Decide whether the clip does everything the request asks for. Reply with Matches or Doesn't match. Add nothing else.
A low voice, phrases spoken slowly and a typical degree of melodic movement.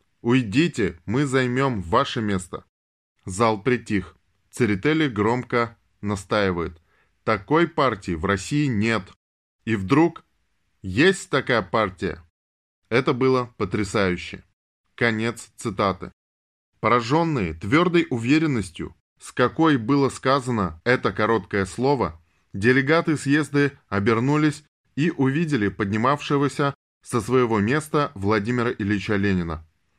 Doesn't match